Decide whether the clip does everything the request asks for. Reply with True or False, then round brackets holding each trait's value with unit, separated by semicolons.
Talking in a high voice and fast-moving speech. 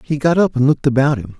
False (140 Hz; 300 wpm)